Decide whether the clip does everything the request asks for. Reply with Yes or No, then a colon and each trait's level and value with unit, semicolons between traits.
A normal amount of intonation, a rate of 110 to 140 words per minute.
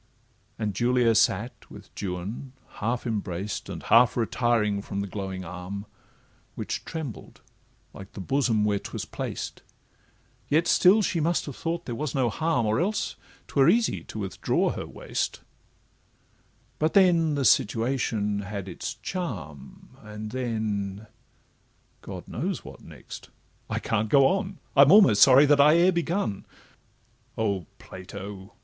No: wide, 6.3 semitones; slow, 135 wpm